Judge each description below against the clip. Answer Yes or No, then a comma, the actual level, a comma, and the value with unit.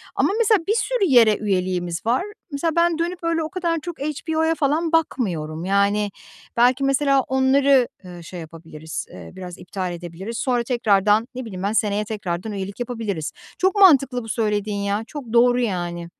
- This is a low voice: No, high, 230 Hz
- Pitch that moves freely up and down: Yes, wide, 7.2 semitones